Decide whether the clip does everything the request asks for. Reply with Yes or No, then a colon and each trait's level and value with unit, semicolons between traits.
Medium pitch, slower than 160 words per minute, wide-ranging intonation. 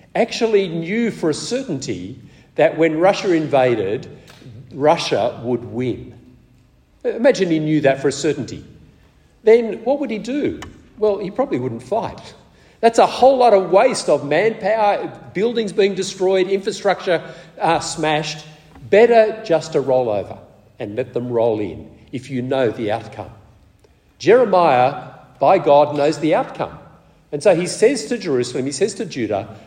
Yes: medium, 160 Hz; average, 150 wpm; wide, 8.1 semitones